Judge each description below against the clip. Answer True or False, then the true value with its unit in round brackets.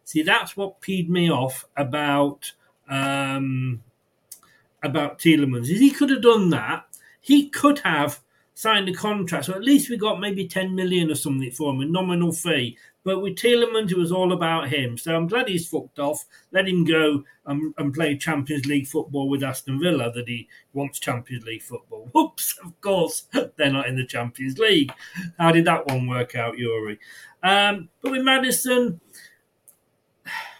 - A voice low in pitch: False (160 Hz)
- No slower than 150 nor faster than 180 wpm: True (175 wpm)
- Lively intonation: True (6.1 semitones)